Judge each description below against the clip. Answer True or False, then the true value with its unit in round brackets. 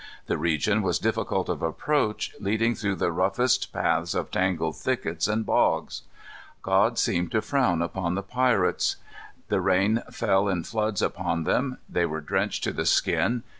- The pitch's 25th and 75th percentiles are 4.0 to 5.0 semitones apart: True (4.7 semitones)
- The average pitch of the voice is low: True (95 Hz)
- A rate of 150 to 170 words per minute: True (160 wpm)